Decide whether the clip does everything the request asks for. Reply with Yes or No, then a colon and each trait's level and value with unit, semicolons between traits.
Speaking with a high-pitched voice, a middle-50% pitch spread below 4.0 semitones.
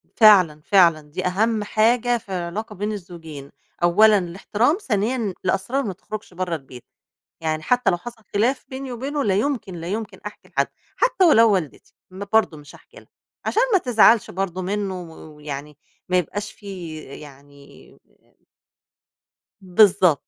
No: high, 195 Hz; average, 4.5 semitones